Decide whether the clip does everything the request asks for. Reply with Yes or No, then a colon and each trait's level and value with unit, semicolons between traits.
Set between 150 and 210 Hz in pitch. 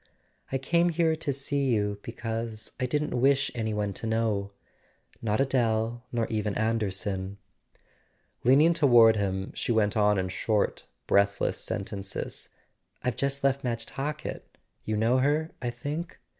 No: low, 115 Hz